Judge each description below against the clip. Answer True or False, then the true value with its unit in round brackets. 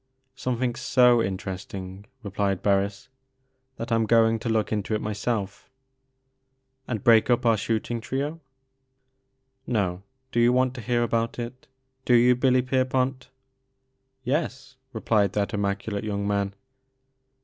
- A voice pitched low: True (120 Hz)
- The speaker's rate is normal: True (150 wpm)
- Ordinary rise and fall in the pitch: True (3.9 semitones)